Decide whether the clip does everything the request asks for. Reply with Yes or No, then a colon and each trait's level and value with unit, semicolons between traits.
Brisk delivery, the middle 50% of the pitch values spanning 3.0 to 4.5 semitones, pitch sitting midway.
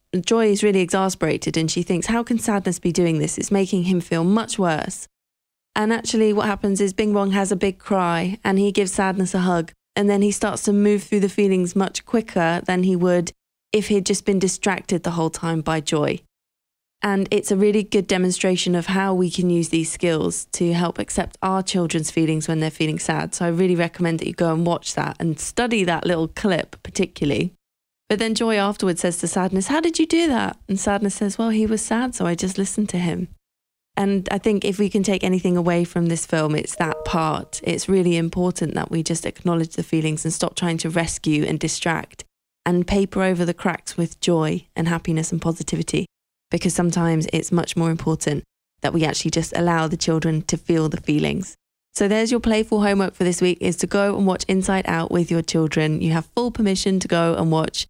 Yes: fast, 215 wpm; average, 3.3 semitones; medium, 180 Hz